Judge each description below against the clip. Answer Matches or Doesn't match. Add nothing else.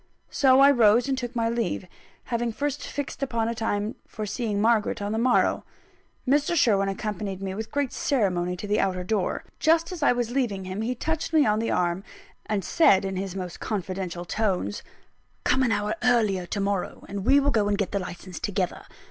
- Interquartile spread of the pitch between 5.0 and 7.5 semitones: Doesn't match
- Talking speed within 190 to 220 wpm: Matches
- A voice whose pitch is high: Matches